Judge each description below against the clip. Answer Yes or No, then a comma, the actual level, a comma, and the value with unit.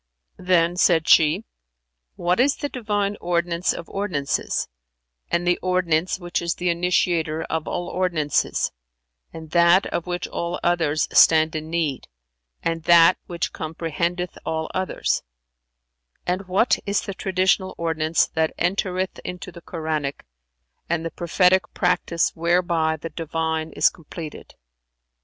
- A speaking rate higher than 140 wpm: No, slow, 135 wpm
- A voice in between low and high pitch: Yes, medium, 170 Hz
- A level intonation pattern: Yes, narrow, 2.1 semitones